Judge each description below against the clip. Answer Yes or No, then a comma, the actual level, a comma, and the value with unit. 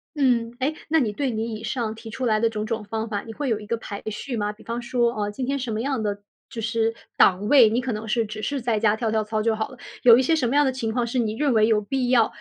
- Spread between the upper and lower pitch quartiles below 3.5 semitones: Yes, average, 2.7 semitones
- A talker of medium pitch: No, high, 230 Hz